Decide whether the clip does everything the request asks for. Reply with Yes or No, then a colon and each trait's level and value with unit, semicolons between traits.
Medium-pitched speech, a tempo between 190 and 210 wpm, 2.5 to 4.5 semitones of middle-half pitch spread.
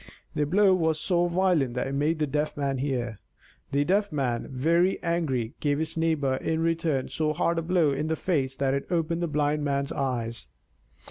Yes: medium, 150 Hz; average, 195 wpm; average, 3.4 semitones